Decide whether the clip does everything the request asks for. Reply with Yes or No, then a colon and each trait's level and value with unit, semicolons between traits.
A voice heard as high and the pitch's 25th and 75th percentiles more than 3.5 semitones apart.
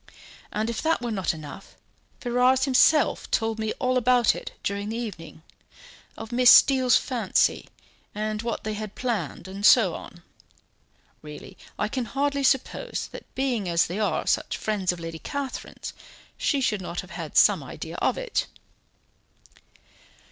Yes: high, 225 Hz; average, 4.3 semitones